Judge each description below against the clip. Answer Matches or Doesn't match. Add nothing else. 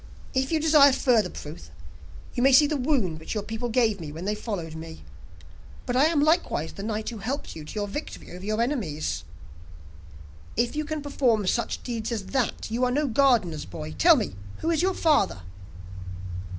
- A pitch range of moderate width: Doesn't match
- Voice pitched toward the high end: Matches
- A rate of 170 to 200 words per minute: Matches